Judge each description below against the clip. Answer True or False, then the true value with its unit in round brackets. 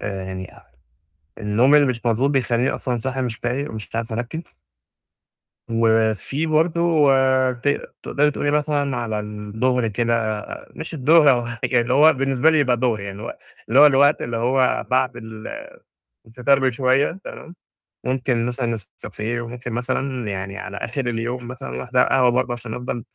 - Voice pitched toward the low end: True (125 Hz)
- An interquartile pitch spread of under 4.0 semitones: True (3.2 semitones)